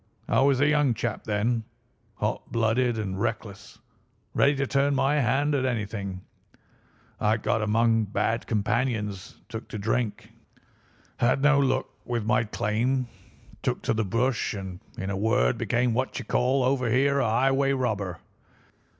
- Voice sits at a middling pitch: No, low, 115 Hz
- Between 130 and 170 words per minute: Yes, average, 155 wpm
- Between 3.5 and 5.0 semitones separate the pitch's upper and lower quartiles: Yes, average, 3.8 semitones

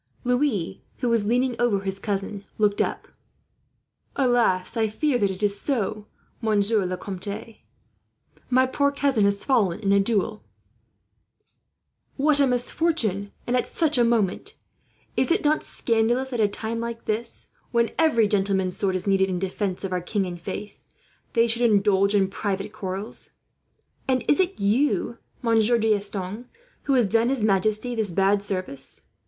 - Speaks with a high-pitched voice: Yes, high, 215 Hz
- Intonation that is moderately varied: Yes, average, 3.6 semitones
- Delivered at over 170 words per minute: No, average, 160 wpm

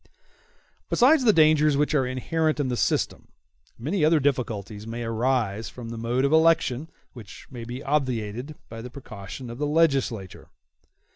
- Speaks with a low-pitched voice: Yes, low, 130 Hz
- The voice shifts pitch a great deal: No, average, 4.7 semitones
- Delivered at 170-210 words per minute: No, average, 155 wpm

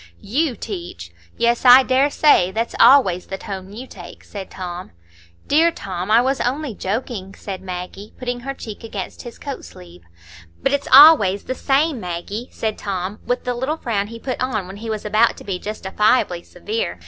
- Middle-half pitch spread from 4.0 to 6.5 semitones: Yes, average, 5.3 semitones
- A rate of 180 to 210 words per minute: Yes, average, 185 wpm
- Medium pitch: No, high, 220 Hz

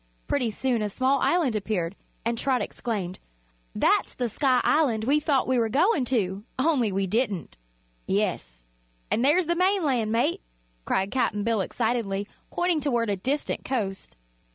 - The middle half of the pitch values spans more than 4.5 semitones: Yes, average, 5.1 semitones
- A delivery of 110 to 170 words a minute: Yes, average, 155 wpm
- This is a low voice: No, high, 235 Hz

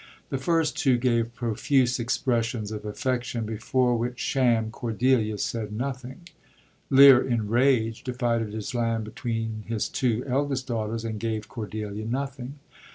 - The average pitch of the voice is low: Yes, low, 120 Hz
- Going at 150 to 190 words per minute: No, slow, 135 wpm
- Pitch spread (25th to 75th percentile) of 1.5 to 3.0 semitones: Yes, narrow, 2.6 semitones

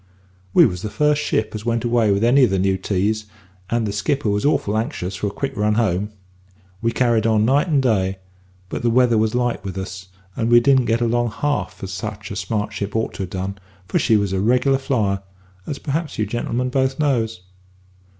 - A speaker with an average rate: No, fast, 215 wpm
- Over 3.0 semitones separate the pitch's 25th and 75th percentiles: Yes, average, 3.7 semitones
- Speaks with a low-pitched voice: Yes, low, 110 Hz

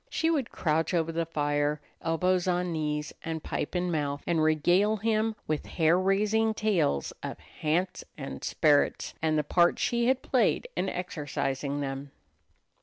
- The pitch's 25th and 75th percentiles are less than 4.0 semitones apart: No, average, 4.3 semitones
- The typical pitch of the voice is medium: Yes, medium, 165 Hz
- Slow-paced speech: No, average, 155 wpm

